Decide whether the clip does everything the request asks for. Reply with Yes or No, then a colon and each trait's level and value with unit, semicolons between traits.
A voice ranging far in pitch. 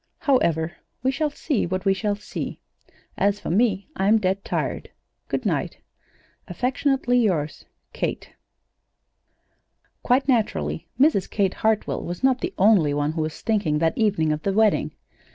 Yes: wide, 6.6 semitones